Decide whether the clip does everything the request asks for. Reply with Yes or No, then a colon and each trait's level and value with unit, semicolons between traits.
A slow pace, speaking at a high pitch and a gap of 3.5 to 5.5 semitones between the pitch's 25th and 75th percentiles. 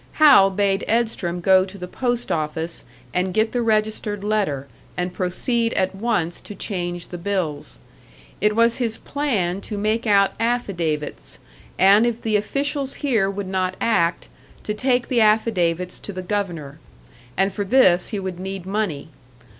No: average, 155 wpm; high, 200 Hz; average, 3.9 semitones